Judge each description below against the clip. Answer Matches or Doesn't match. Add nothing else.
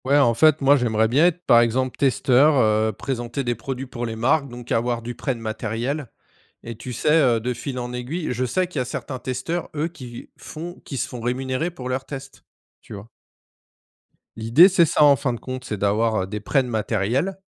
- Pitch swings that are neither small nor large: Matches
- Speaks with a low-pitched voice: Matches